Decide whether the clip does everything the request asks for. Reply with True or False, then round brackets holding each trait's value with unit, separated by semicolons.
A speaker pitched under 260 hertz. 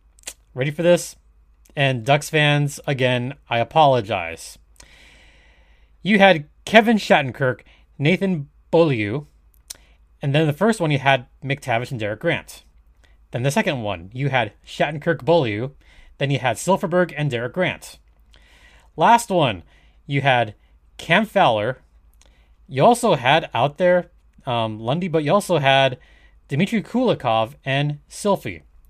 True (135 Hz)